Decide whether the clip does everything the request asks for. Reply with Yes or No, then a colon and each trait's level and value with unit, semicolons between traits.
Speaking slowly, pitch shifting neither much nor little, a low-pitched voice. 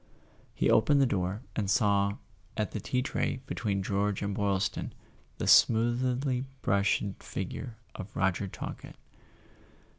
Yes: slow, 125 wpm; average, 3.6 semitones; low, 105 Hz